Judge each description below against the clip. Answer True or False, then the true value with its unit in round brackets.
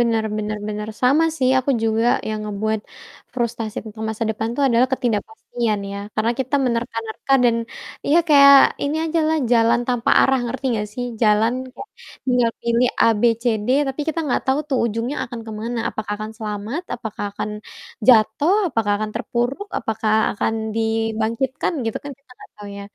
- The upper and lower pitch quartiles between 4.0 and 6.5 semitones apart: False (2.6 semitones)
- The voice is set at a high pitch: True (230 Hz)